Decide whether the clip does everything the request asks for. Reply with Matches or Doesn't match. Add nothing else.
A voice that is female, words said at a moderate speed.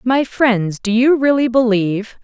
Matches